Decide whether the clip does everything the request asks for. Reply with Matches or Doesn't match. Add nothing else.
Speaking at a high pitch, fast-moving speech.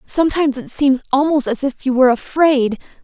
Doesn't match